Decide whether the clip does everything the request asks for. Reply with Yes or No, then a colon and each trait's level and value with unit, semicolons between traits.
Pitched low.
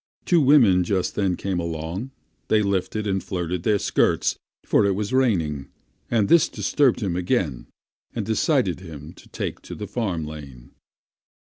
Yes: very low, 95 Hz